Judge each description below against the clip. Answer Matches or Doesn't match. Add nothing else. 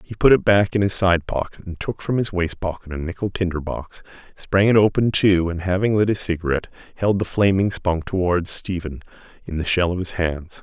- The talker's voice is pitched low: Matches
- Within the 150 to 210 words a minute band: Matches